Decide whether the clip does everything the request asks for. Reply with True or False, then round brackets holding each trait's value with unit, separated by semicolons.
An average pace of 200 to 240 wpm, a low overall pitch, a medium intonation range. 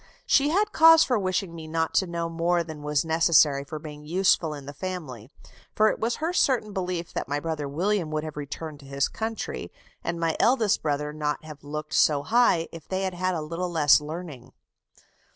False (205 wpm; 165 Hz; 4.0 semitones)